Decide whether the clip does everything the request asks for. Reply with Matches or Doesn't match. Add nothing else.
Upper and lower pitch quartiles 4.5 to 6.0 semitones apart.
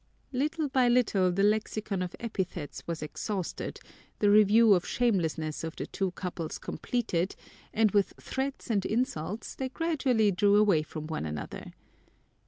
Matches